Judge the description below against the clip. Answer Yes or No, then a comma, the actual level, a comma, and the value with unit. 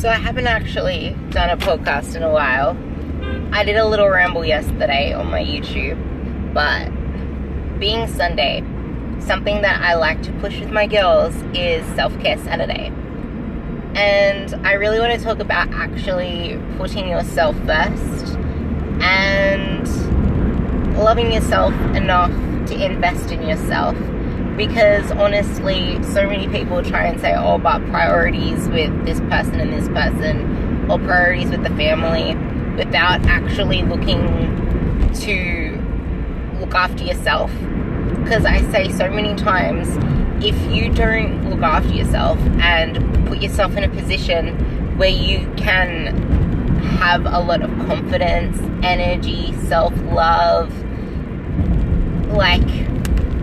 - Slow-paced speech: Yes, slow, 125 wpm